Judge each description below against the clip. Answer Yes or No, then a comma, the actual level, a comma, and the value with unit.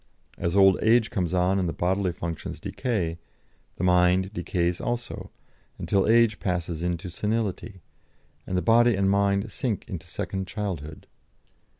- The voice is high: No, very low, 95 Hz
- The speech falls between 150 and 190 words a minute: No, slow, 135 wpm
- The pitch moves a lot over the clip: No, average, 3.1 semitones